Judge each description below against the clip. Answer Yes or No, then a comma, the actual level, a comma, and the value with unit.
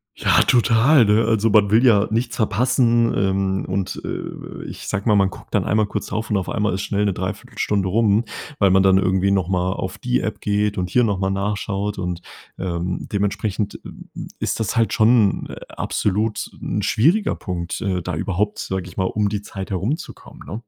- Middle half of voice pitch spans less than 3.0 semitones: Yes, narrow, 2.5 semitones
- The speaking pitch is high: No, low, 100 Hz